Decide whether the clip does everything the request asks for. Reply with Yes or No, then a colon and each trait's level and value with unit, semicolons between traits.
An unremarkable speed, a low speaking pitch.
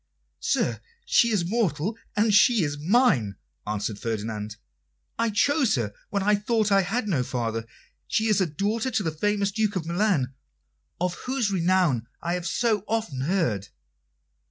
No: average, 155 wpm; high, 190 Hz